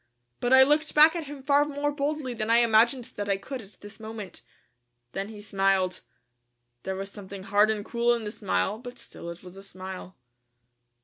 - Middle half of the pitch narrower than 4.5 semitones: No, average, 5.2 semitones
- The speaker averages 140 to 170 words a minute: No, average, 195 wpm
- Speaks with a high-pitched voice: Yes, high, 220 Hz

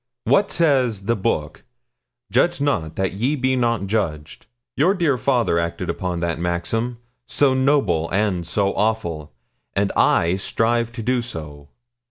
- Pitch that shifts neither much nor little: No, wide, 6.7 semitones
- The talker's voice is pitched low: Yes, low, 110 Hz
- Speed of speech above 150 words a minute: No, average, 145 wpm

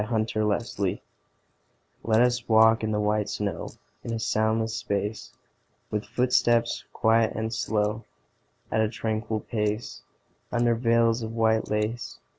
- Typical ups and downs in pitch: No, narrow, 1.3 semitones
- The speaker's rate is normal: No, slow, 130 wpm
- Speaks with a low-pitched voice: Yes, low, 110 Hz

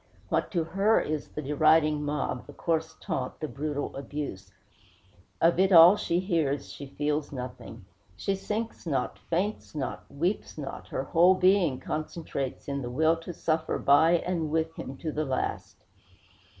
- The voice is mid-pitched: Yes, medium, 155 Hz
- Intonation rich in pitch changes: No, average, 3.3 semitones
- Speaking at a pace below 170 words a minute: Yes, average, 160 wpm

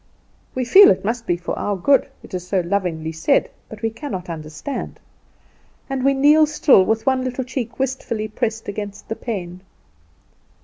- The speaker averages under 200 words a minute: Yes, average, 170 wpm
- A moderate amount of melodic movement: No, wide, 6.0 semitones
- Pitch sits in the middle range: No, high, 220 Hz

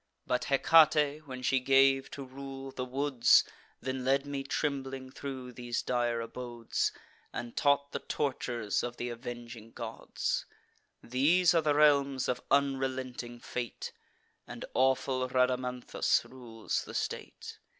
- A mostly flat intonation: Yes, narrow, 2.1 semitones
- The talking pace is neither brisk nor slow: No, slow, 130 wpm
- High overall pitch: No, low, 130 Hz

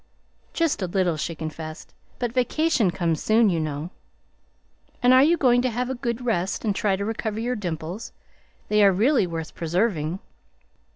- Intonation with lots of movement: Yes, wide, 6.3 semitones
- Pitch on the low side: No, high, 205 Hz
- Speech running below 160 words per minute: No, average, 170 wpm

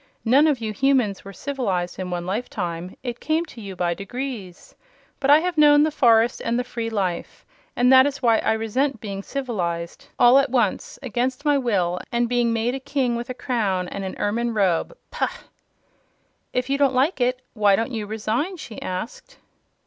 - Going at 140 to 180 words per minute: No, average, 190 wpm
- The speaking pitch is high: Yes, high, 235 Hz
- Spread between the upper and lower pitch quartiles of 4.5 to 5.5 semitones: Yes, average, 5.1 semitones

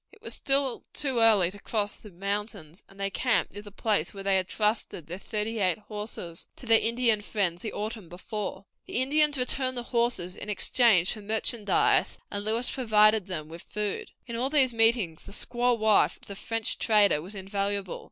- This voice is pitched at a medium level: No, high, 210 Hz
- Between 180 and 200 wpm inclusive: Yes, average, 190 wpm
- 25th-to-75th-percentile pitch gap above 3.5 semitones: No, average, 3.1 semitones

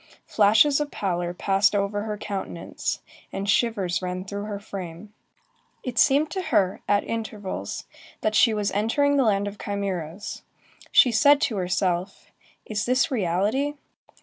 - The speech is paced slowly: No, average, 145 wpm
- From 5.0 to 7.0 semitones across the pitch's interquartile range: No, average, 3.2 semitones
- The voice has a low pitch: No, high, 205 Hz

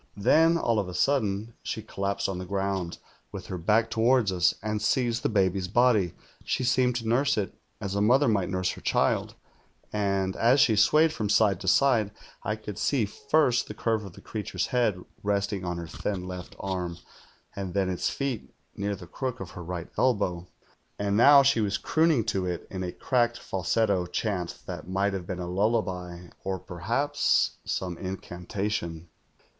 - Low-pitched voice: Yes, low, 100 Hz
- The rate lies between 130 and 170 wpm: No, average, 180 wpm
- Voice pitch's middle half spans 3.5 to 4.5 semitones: Yes, average, 4.2 semitones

